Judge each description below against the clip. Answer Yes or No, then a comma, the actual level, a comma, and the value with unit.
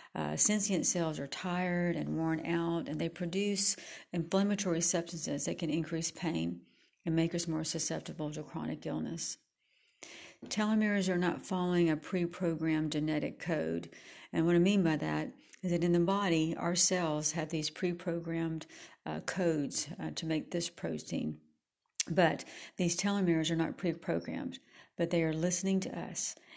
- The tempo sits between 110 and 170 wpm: Yes, average, 150 wpm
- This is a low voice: No, medium, 170 Hz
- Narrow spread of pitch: Yes, narrow, 1.9 semitones